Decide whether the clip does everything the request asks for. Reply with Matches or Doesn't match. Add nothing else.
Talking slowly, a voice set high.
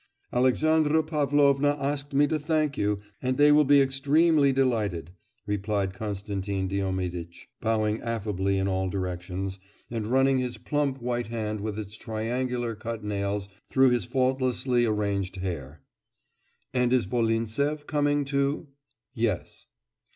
Doesn't match